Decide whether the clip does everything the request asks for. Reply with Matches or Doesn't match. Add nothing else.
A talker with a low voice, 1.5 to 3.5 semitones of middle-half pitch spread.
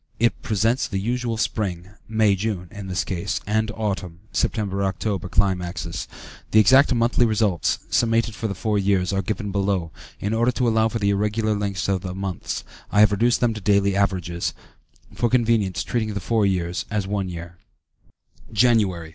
Matches